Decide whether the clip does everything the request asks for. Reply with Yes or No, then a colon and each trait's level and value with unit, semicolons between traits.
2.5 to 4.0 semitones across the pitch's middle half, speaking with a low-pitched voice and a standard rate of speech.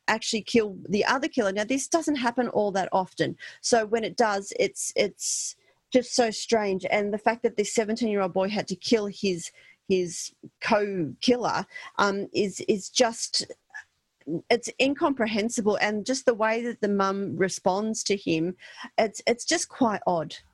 No: average, 3.3 semitones; high, 220 Hz; average, 170 wpm